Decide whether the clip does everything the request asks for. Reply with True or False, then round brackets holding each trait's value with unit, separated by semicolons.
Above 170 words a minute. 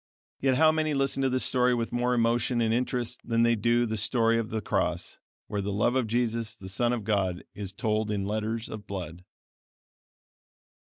True (200 wpm)